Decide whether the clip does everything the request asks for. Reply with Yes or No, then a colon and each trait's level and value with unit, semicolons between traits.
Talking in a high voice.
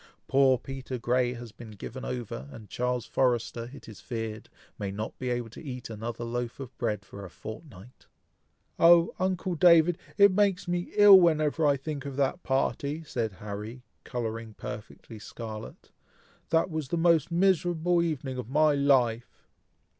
No: low, 130 Hz